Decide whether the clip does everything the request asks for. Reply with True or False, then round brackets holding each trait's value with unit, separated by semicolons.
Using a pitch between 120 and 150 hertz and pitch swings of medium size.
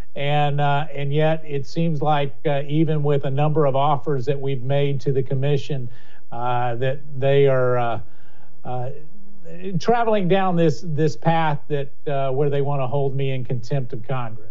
False (140 Hz; 2.2 semitones)